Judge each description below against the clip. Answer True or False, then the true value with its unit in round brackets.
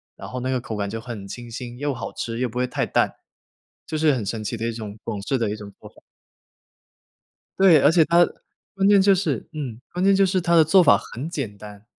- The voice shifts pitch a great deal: True (6.7 semitones)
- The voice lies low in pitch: True (125 Hz)